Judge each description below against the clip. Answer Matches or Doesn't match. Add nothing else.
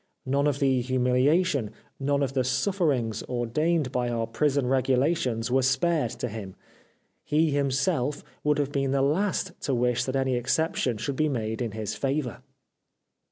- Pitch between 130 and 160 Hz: Matches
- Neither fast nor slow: Matches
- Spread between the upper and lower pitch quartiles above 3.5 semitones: Doesn't match